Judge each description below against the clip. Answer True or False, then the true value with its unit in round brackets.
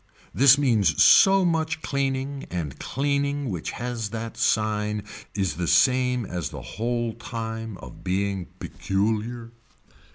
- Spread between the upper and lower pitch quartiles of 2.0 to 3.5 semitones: False (5.0 semitones)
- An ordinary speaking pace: False (125 wpm)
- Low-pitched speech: True (115 Hz)